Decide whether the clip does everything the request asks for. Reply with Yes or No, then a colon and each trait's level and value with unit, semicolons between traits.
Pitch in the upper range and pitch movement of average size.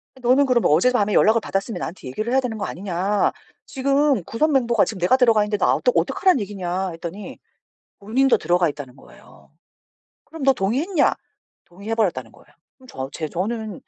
No: high, 215 Hz; wide, 6.1 semitones